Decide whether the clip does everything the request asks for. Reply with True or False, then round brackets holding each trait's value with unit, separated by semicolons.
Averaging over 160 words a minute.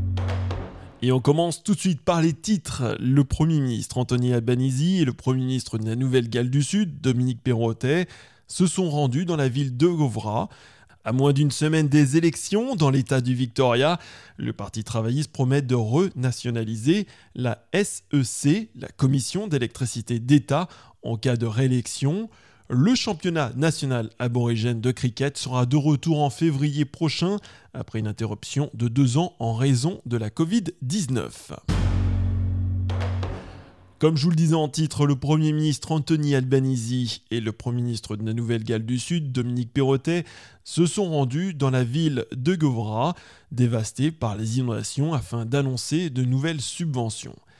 False (155 wpm)